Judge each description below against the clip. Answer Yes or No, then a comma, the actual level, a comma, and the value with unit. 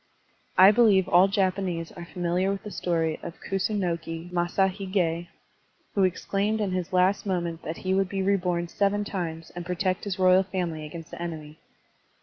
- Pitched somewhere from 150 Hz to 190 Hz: Yes, medium, 185 Hz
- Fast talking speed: No, average, 160 wpm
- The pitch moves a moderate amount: No, narrow, 2.2 semitones